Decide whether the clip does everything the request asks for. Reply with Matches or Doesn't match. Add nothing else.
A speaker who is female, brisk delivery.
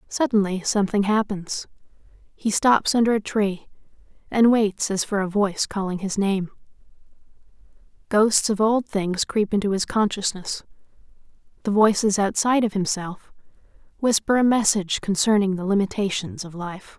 Doesn't match